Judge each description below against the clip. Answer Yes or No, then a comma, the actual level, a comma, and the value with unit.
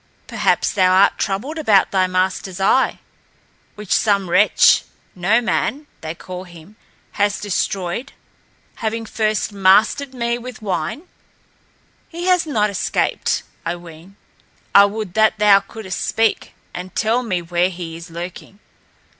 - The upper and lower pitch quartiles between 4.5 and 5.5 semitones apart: No, average, 3.5 semitones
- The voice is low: No, high, 200 Hz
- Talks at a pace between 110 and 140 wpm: Yes, slow, 135 wpm